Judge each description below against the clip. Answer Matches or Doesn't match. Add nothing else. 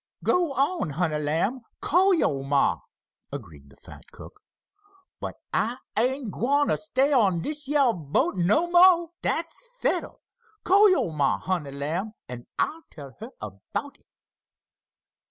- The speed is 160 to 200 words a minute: Doesn't match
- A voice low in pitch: Doesn't match